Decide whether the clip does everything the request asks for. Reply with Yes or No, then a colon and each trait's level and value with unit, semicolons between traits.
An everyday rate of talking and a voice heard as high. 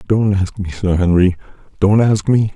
No: average, 165 wpm; low, 100 Hz